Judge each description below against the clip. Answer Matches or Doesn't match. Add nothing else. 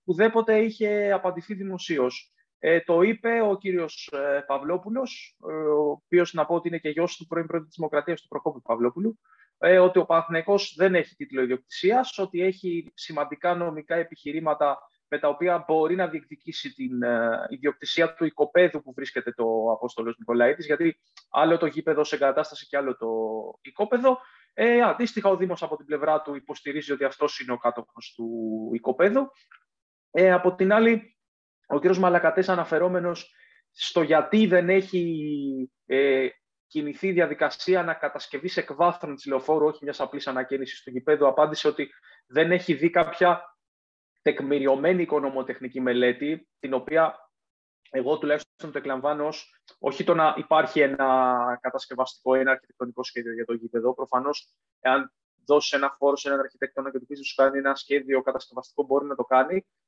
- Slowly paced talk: Doesn't match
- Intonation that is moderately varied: Matches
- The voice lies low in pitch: Doesn't match